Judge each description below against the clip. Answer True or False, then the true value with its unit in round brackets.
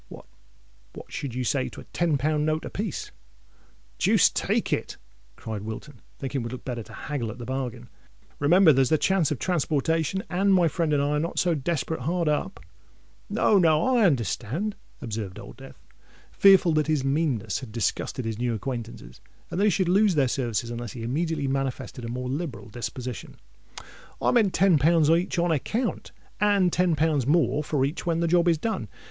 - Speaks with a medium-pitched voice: True (150 Hz)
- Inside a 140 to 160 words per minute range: False (185 wpm)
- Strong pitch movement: True (5.8 semitones)